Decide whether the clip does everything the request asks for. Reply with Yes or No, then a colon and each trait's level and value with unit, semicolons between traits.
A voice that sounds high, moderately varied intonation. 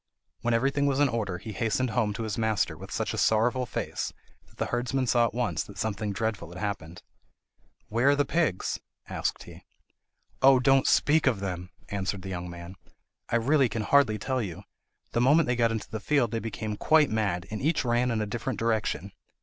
No: low, 115 Hz; average, 4.0 semitones